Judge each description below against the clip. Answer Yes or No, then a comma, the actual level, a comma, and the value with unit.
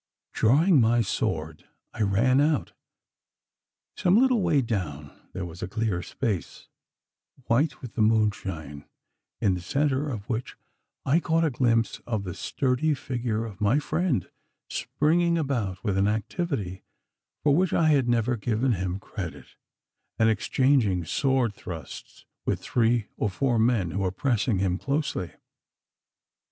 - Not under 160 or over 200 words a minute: No, average, 140 wpm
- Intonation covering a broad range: Yes, wide, 6.0 semitones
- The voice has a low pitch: Yes, low, 115 Hz